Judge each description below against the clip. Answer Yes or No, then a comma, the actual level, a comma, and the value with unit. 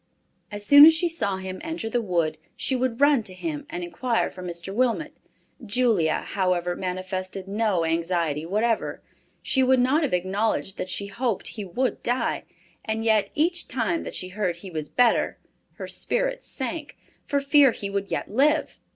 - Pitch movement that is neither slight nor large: No, wide, 6.1 semitones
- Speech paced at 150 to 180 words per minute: Yes, average, 175 wpm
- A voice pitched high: Yes, high, 220 Hz